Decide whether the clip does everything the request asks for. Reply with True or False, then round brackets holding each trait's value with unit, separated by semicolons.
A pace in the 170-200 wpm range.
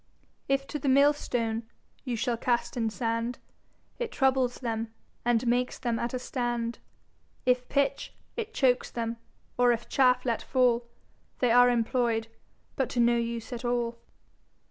False (155 wpm)